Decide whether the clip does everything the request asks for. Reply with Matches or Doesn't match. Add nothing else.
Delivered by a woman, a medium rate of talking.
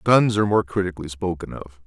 Doesn't match